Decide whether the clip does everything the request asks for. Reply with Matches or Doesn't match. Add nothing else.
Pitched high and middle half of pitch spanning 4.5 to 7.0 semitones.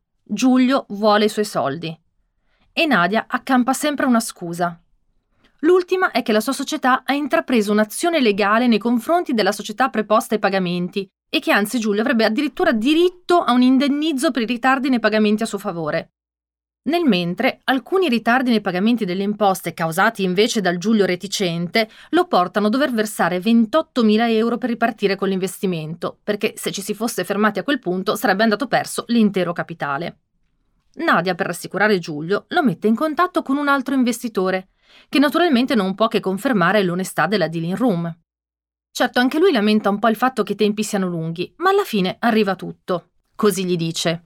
Matches